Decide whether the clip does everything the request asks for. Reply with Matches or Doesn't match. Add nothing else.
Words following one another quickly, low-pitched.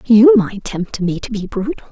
Doesn't match